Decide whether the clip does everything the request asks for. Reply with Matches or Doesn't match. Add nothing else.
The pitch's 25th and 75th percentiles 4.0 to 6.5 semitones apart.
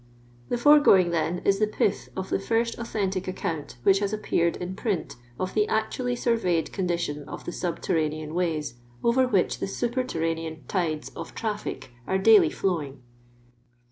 Matches